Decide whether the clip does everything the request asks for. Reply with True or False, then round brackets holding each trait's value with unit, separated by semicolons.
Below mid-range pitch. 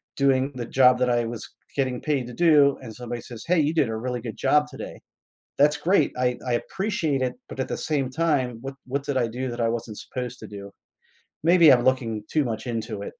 True (130 Hz)